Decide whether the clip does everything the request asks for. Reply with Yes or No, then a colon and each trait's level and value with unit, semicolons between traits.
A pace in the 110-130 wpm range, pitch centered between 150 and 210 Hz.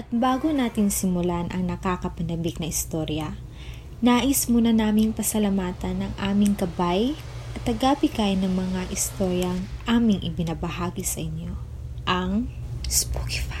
Yes: average, 115 wpm; medium, 185 Hz